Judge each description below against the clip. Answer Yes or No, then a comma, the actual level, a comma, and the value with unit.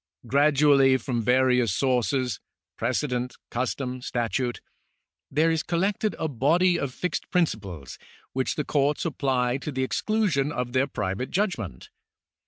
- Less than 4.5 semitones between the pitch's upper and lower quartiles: Yes, average, 3.5 semitones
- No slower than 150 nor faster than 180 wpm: No, average, 140 wpm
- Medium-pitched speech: No, low, 130 Hz